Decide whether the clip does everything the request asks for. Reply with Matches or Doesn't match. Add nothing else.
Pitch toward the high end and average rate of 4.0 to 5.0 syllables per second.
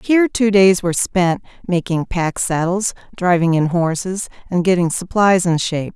Doesn't match